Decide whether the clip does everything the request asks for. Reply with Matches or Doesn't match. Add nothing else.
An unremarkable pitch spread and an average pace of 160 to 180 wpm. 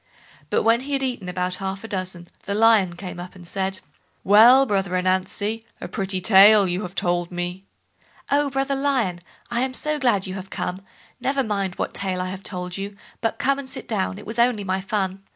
Doesn't match